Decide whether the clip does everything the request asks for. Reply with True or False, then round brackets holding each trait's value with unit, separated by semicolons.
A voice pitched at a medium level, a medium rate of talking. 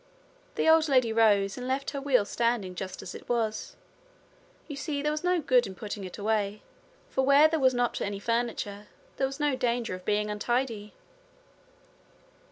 False (240 Hz; 175 wpm)